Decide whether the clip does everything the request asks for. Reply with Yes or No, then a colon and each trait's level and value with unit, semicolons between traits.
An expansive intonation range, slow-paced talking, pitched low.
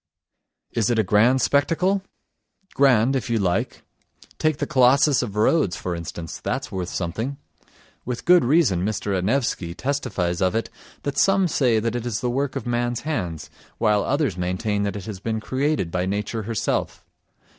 No: wide, 5.9 semitones; average, 165 wpm; low, 115 Hz